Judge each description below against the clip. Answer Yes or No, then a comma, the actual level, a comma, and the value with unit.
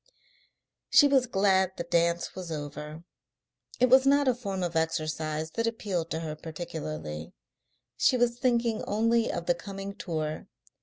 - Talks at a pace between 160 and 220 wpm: No, average, 150 wpm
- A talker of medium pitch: Yes, medium, 180 Hz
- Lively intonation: Yes, wide, 6.4 semitones